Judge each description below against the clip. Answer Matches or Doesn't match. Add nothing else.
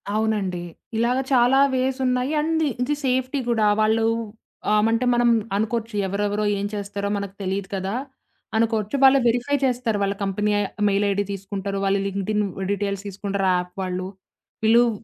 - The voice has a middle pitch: Doesn't match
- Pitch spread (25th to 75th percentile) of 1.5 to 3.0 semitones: Doesn't match